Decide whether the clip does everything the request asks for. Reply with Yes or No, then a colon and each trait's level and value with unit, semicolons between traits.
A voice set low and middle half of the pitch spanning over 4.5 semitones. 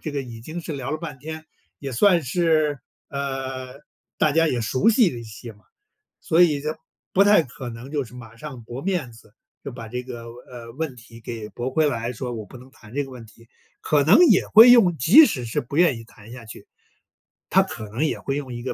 Yes: low, 130 Hz; average, 4.9 semitones